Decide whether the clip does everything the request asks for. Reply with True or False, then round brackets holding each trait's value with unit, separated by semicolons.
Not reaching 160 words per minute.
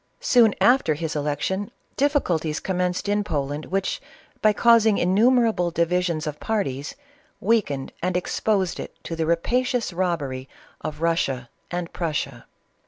True (135 wpm)